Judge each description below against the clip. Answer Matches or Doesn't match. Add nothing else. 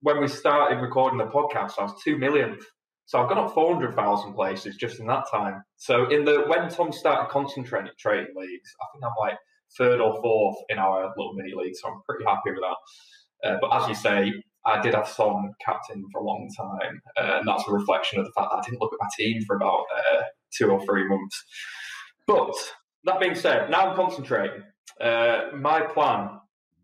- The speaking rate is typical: Doesn't match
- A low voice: Doesn't match